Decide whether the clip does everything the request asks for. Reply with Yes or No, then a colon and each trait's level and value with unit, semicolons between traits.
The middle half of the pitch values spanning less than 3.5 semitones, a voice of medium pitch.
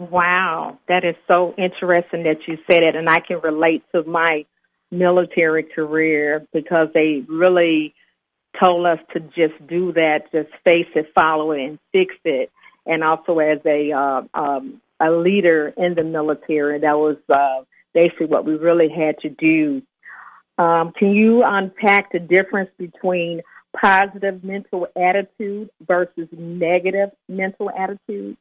Yes: average, 3.1 semitones; medium, 170 Hz